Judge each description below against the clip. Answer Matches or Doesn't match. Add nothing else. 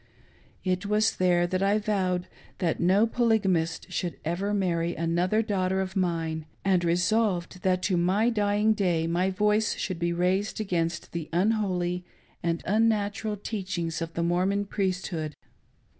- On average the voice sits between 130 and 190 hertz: Matches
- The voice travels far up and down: Doesn't match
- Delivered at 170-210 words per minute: Doesn't match